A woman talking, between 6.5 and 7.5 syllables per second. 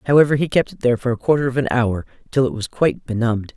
Yes: female; 7.4 syllables/s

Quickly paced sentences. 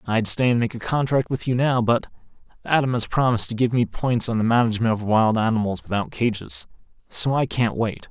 Yes: fast, 215 wpm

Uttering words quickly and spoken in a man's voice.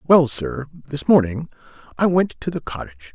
No: average, 170 wpm; male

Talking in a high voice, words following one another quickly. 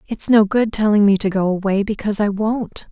Yes: high, 205 Hz; fast, 225 wpm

